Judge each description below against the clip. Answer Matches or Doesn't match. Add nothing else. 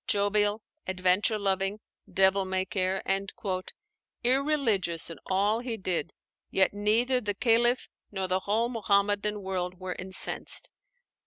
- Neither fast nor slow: Doesn't match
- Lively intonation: Doesn't match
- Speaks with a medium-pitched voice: Doesn't match